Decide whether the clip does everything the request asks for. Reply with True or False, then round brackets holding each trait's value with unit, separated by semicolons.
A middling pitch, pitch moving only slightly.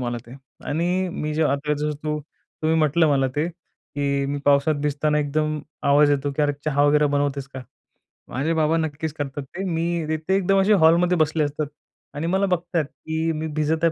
True (155 Hz; 2.3 semitones)